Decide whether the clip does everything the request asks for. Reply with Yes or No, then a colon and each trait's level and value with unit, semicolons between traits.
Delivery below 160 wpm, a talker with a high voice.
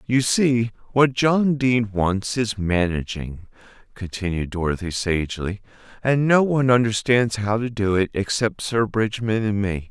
No: average, 145 wpm; low, 110 Hz